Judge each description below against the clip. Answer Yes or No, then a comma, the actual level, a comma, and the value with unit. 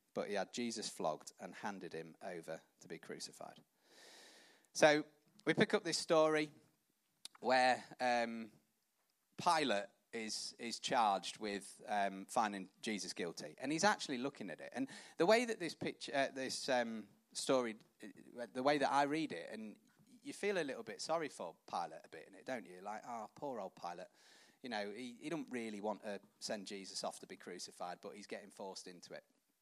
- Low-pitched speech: Yes, low, 125 Hz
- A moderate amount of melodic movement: No, wide, 7.1 semitones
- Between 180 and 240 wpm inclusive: Yes, average, 185 wpm